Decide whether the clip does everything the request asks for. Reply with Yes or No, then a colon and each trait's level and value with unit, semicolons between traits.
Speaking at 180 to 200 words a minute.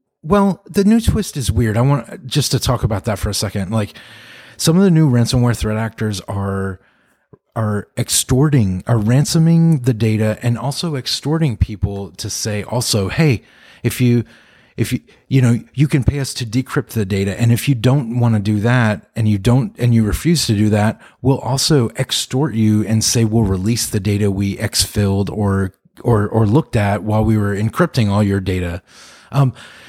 Yes: average, 195 wpm